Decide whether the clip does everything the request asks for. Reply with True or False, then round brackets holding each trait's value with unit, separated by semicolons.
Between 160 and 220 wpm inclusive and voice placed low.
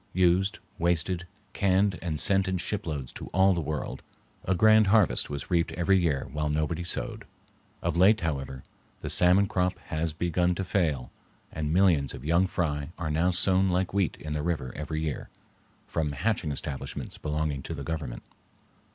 True (170 wpm; 85 Hz)